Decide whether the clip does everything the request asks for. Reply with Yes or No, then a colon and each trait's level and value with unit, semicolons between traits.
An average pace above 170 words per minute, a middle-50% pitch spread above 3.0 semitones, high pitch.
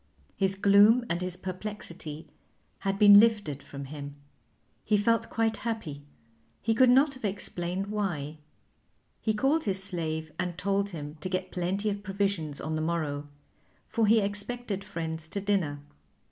No: average, 150 wpm; average, 4.6 semitones; high, 195 Hz